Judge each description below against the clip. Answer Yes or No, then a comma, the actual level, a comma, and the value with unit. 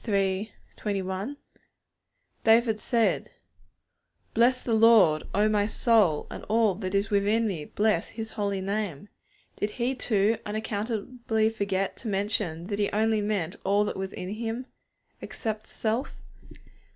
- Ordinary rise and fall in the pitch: No, narrow, 2.0 semitones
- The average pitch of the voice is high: Yes, high, 215 Hz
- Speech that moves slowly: Yes, slow, 125 wpm